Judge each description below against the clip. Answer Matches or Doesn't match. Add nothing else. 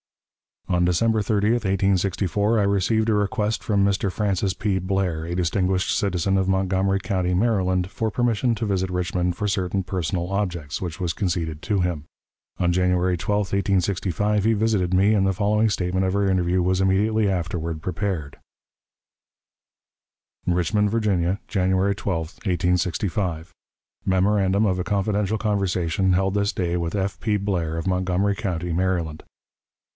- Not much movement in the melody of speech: Matches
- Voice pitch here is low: Matches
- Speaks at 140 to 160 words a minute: Matches